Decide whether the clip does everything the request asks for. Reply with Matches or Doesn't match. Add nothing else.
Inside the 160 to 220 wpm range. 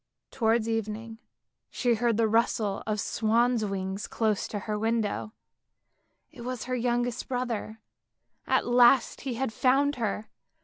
Doesn't match